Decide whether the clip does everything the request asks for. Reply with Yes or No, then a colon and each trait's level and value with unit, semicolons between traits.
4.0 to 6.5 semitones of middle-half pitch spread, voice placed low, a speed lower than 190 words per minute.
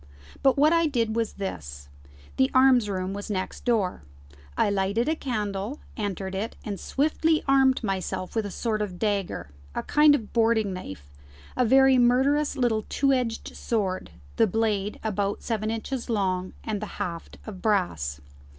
No: average, 4.5 semitones; high, 215 Hz; average, 160 wpm